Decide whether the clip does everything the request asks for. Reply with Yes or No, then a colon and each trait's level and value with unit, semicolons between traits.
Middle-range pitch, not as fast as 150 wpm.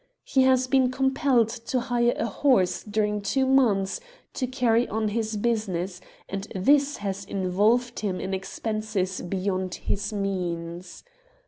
No: high, 215 Hz; average, 140 wpm